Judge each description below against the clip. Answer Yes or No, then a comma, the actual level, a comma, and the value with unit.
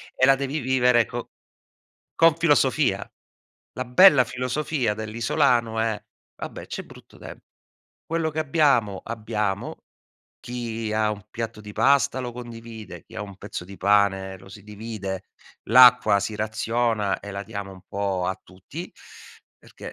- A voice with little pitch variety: No, average, 3.7 semitones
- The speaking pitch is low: Yes, low, 115 Hz